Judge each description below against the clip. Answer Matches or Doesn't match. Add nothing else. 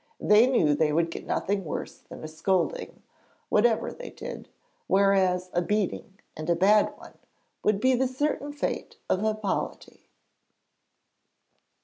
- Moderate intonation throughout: Matches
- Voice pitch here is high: Matches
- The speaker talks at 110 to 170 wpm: Matches